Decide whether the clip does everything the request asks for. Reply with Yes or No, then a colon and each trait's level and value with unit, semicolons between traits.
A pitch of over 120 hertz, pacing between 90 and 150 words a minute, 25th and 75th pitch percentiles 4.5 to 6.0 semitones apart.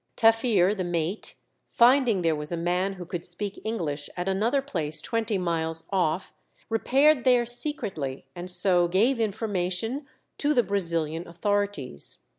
Yes: high, 190 Hz; average, 140 wpm; average, 4.9 semitones